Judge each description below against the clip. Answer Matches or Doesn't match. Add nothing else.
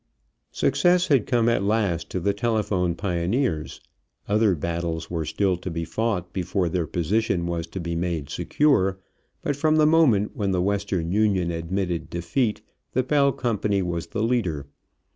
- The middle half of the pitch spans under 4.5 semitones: Doesn't match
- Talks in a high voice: Doesn't match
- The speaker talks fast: Doesn't match